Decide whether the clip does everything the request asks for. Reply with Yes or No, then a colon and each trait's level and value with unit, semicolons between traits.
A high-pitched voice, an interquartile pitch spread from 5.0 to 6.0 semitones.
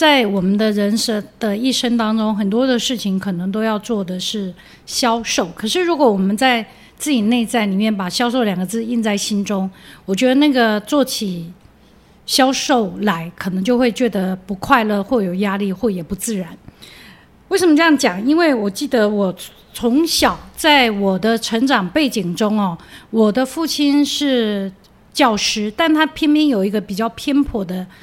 No: high, 225 Hz; average, 4.5 semitones